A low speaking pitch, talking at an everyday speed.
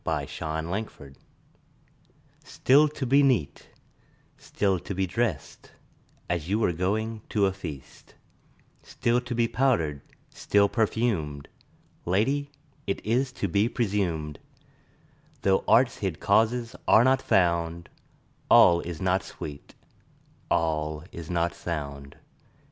No: very low, 95 Hz; slow, 120 wpm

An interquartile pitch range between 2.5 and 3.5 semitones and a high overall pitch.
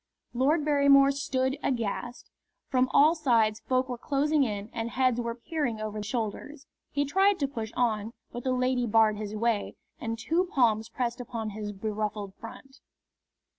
No: average, 3.9 semitones; high, 245 Hz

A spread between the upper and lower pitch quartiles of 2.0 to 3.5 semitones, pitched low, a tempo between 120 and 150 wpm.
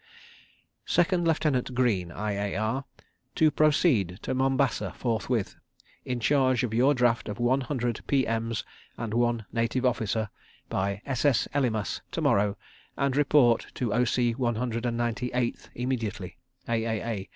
Yes: average, 2.9 semitones; low, 120 Hz; slow, 135 wpm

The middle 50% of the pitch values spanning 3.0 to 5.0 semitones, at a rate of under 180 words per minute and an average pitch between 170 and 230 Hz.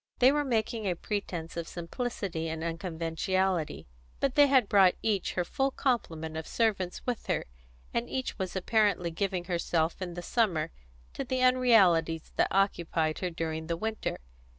No: wide, 5.4 semitones; average, 160 wpm; medium, 185 Hz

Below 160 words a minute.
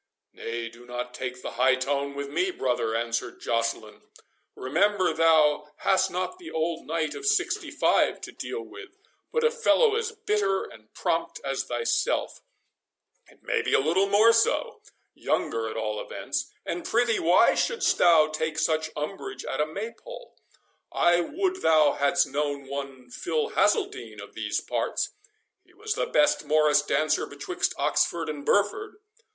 Yes: average, 150 wpm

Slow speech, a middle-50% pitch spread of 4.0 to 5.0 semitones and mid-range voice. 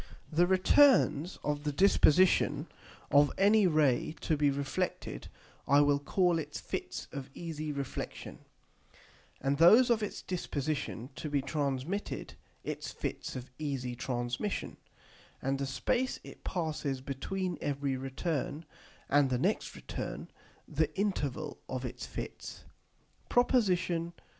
Yes: slow, 125 wpm; average, 4.7 semitones; medium, 150 Hz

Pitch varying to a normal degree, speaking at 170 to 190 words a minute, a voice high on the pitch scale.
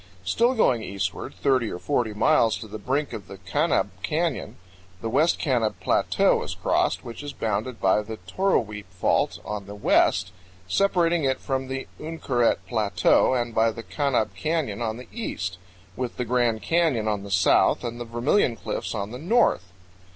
No: average, 4.7 semitones; average, 175 wpm; low, 120 Hz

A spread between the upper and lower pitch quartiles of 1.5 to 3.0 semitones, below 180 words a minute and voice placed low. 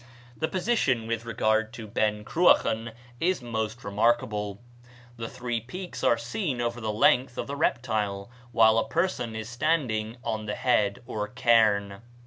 Yes: narrow, 2.4 semitones; average, 150 wpm; low, 115 Hz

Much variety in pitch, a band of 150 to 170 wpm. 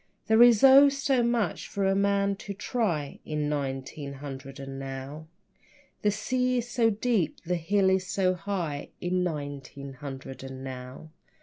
Yes: wide, 7.0 semitones; average, 160 wpm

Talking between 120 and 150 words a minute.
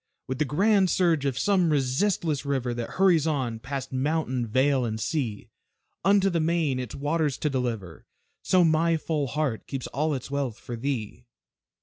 No: average, 165 wpm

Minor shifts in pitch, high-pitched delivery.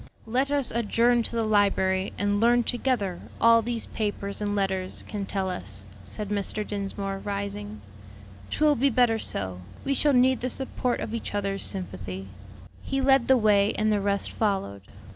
No: average, 3.5 semitones; high, 205 Hz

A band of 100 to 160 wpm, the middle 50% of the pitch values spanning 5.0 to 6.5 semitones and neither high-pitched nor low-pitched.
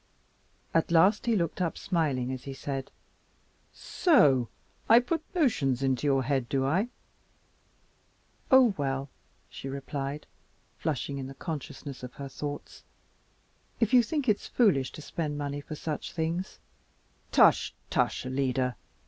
Yes: average, 140 wpm; average, 5.3 semitones; medium, 145 Hz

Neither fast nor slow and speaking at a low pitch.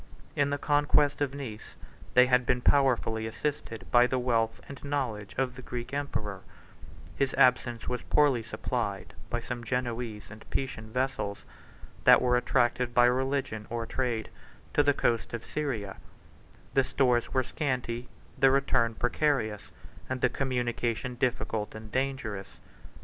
Yes: average, 145 wpm; low, 125 Hz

